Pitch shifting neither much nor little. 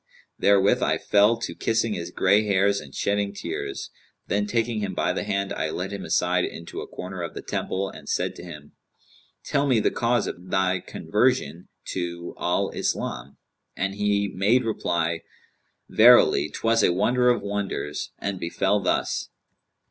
Yes: average, 3.0 semitones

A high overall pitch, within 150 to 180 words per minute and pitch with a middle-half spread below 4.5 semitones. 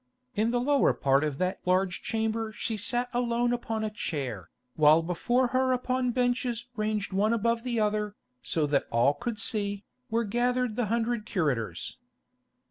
No: high, 220 Hz; average, 160 wpm; average, 4.8 semitones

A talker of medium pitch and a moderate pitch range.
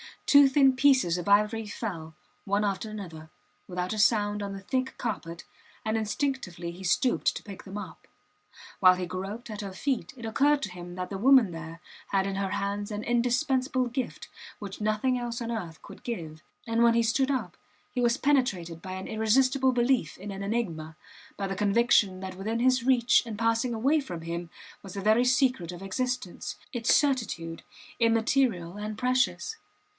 No: high, 215 Hz; average, 4.8 semitones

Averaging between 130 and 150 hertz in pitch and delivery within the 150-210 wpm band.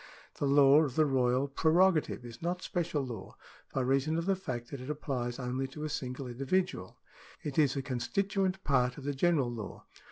Yes: medium, 140 Hz; average, 190 wpm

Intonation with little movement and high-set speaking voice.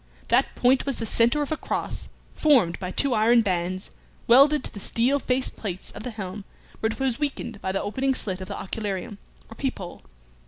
No: wide, 5.4 semitones; high, 225 Hz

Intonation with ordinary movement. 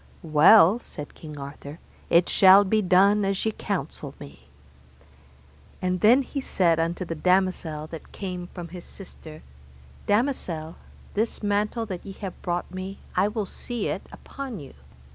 Yes: average, 3.7 semitones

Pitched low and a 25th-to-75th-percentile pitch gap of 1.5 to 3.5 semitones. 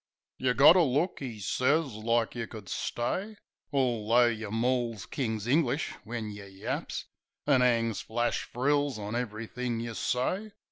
Yes: low, 120 Hz; average, 3.2 semitones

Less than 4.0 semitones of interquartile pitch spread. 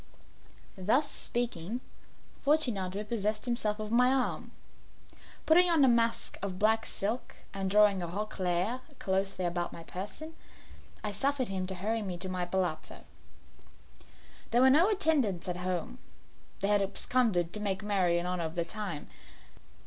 No: average, 4.7 semitones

